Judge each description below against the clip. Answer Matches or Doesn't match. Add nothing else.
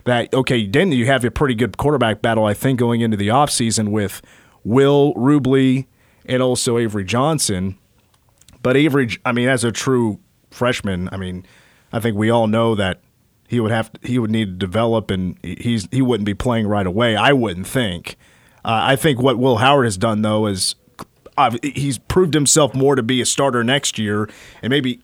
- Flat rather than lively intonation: Doesn't match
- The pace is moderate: Matches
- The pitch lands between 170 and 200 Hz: Doesn't match